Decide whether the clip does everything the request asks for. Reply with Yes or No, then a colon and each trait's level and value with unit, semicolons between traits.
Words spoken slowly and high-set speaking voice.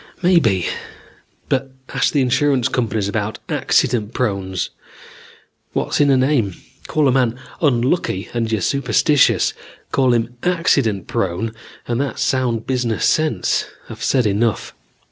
No: slow, 125 wpm; low, 120 Hz